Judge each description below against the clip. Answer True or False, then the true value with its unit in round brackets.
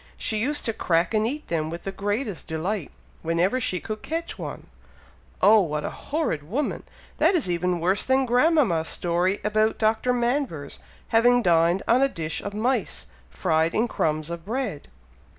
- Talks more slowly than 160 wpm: False (170 wpm)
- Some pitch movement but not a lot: False (6.5 semitones)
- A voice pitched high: True (205 Hz)